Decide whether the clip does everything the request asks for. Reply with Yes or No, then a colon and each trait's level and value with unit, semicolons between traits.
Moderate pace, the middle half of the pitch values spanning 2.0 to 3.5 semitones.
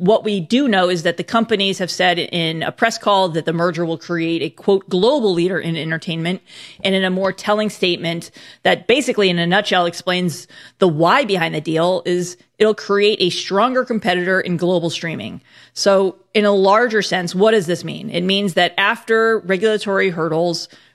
Yes: average, 190 wpm; average, 2.9 semitones